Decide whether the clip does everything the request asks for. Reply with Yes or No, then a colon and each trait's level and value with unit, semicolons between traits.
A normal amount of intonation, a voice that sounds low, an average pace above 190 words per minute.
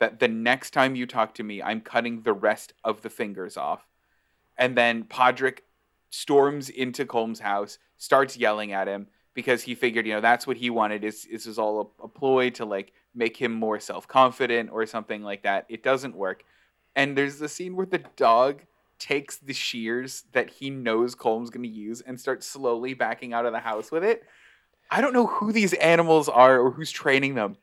Yes: average, 3.2 semitones; low, 120 Hz; average, 200 wpm